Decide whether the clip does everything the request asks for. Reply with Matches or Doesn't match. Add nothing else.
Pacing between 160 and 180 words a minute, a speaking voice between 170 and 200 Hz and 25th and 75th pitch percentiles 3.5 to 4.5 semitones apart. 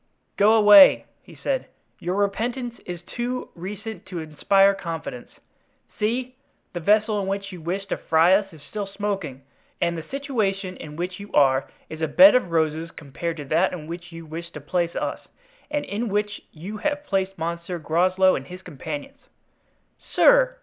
Matches